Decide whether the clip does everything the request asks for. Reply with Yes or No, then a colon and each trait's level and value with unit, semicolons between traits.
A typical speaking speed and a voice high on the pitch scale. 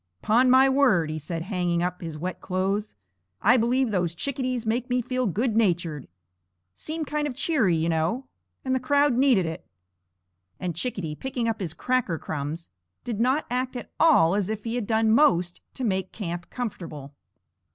Yes: average, 175 wpm; high, 220 Hz